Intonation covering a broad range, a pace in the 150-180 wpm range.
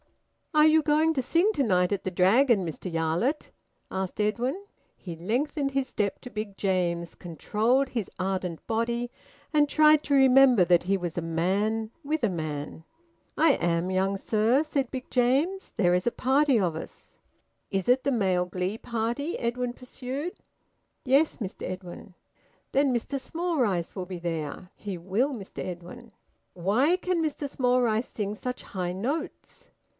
Yes: wide, 6.9 semitones; average, 160 wpm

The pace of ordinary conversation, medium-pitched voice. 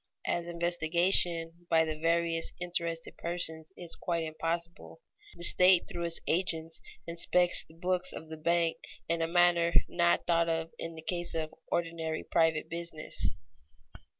Yes: average, 145 wpm; medium, 170 Hz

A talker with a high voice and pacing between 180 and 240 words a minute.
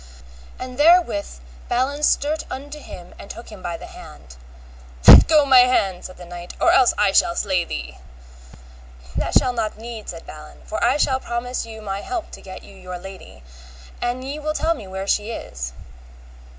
Yes: high, 220 Hz; average, 185 wpm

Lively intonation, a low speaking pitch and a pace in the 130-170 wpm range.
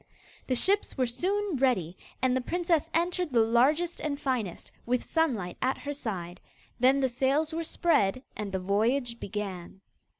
No: wide, 6.5 semitones; very high, 255 Hz; average, 160 wpm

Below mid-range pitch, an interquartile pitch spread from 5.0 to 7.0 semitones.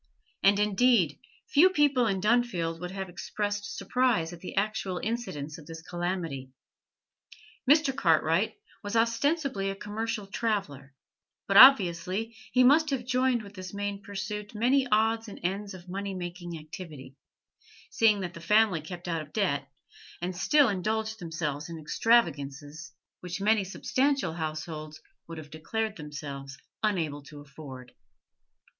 No: high, 195 Hz; wide, 5.5 semitones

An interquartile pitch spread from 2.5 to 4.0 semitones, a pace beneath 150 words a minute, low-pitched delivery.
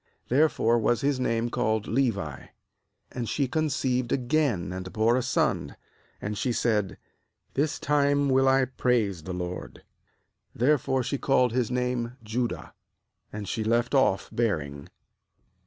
Yes: average, 3.6 semitones; average, 140 wpm; low, 120 Hz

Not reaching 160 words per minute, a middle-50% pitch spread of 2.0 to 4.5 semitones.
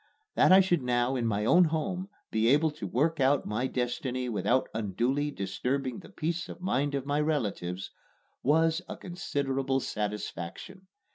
No: average, 150 wpm; average, 5.2 semitones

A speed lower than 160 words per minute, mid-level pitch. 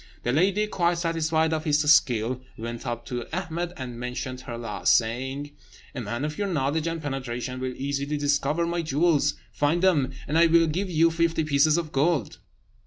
No: average, 180 wpm; medium, 150 Hz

